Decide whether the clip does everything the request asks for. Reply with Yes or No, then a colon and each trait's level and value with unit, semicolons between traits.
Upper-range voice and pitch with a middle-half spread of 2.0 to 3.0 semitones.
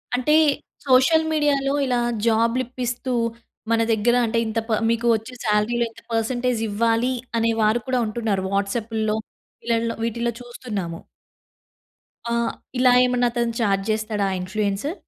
Yes: high, 230 Hz; narrow, 2.4 semitones